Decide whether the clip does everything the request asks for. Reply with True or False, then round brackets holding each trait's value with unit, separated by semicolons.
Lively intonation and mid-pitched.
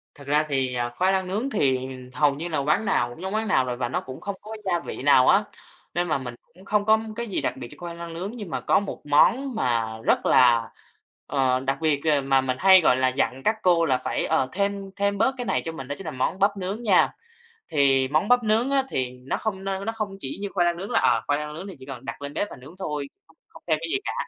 True (6.9 semitones; 160 Hz)